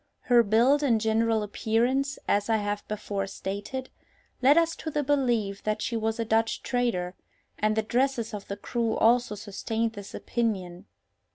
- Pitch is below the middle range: No, high, 225 Hz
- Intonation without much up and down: No, average, 3.0 semitones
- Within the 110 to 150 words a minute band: No, average, 165 wpm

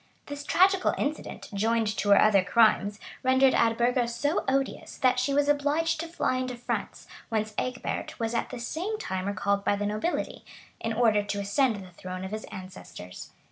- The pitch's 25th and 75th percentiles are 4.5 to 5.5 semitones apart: Yes, average, 5.1 semitones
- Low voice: No, high, 235 Hz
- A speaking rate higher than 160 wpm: Yes, average, 180 wpm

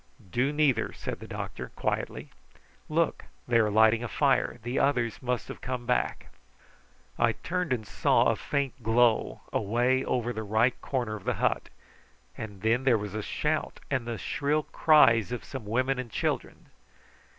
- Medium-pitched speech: No, low, 120 Hz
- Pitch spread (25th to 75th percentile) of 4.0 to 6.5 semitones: No, average, 3.2 semitones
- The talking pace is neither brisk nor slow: Yes, average, 165 wpm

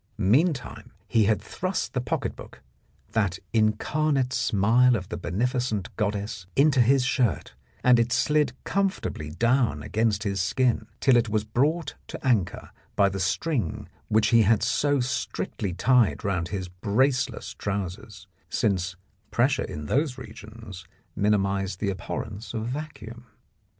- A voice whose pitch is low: Yes, low, 110 Hz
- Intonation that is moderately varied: Yes, average, 4.3 semitones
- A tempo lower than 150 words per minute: Yes, average, 140 wpm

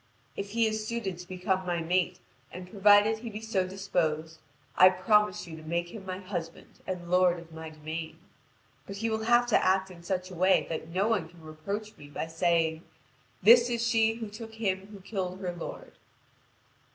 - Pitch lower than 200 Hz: Yes, medium, 185 Hz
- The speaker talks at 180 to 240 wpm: Yes, average, 195 wpm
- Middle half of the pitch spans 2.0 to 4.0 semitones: Yes, average, 3.7 semitones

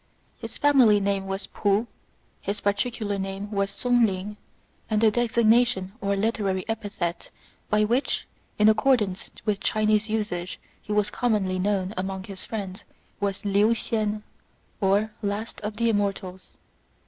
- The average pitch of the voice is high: Yes, high, 205 Hz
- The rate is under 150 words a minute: Yes, average, 140 wpm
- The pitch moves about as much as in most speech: No, narrow, 2.0 semitones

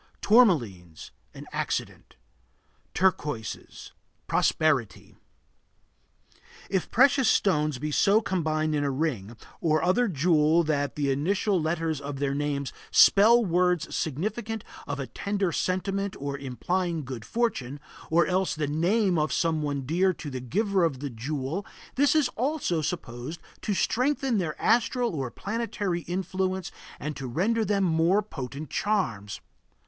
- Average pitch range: No, wide, 5.7 semitones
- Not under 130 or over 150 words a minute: Yes, slow, 135 wpm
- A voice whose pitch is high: No, medium, 165 Hz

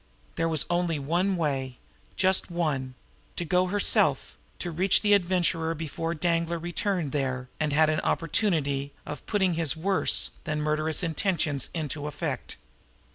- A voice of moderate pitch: Yes, medium, 165 Hz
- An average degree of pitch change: Yes, average, 3.1 semitones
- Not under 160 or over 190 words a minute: No, average, 145 wpm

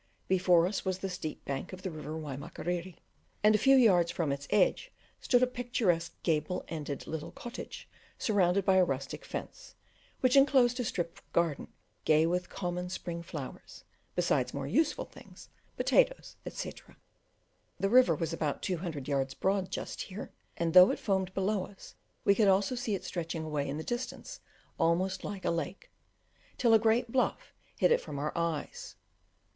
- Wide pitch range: No, average, 4.6 semitones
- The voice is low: No, medium, 180 Hz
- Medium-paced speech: Yes, average, 175 wpm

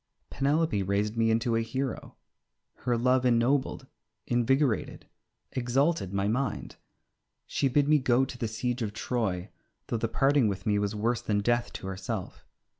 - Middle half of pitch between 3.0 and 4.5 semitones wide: Yes, average, 3.6 semitones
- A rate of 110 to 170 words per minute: Yes, average, 155 wpm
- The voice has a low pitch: Yes, low, 120 Hz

